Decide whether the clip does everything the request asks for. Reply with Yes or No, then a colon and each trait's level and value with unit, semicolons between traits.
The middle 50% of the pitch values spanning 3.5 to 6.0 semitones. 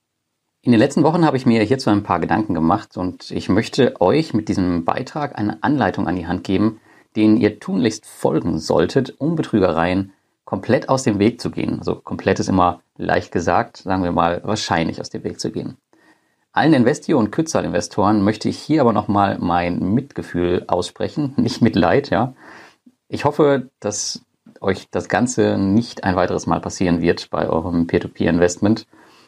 Yes: average, 4.1 semitones